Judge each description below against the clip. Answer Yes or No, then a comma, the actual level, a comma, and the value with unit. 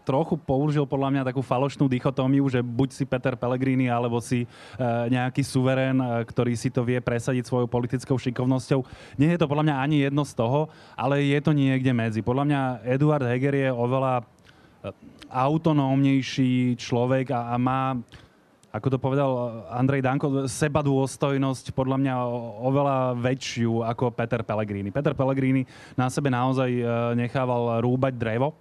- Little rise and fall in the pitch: Yes, narrow, 2.0 semitones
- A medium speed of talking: Yes, average, 145 wpm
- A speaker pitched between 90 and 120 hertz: No, low, 130 Hz